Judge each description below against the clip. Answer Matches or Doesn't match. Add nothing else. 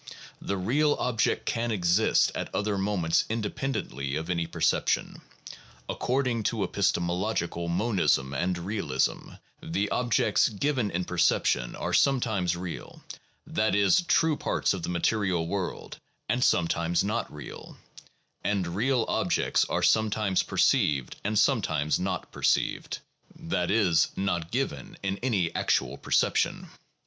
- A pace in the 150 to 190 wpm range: Doesn't match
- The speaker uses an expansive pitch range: Doesn't match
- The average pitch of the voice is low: Matches